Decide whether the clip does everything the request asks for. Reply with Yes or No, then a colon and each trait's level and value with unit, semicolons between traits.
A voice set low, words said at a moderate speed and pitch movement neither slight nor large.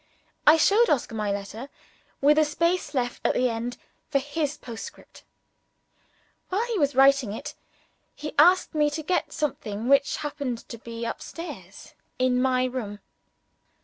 No: very high, 275 Hz; average, 150 wpm; average, 4.0 semitones